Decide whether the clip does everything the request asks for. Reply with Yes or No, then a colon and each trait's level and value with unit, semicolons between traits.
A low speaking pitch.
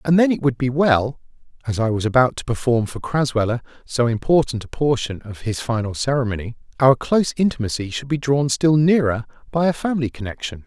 Yes: low, 130 Hz